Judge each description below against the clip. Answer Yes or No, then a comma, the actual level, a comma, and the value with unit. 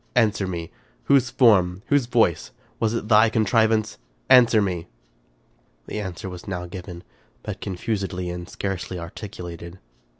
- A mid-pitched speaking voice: No, low, 100 Hz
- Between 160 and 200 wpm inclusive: No, average, 145 wpm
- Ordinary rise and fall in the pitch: Yes, average, 4.0 semitones